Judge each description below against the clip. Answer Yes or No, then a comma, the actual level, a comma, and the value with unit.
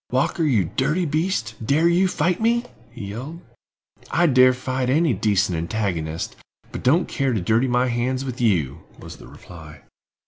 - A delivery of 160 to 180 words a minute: Yes, average, 165 wpm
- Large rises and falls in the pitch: Yes, wide, 6.8 semitones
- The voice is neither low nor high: No, low, 125 Hz